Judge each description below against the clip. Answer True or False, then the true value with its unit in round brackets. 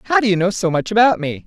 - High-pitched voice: True (200 Hz)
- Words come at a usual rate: False (330 wpm)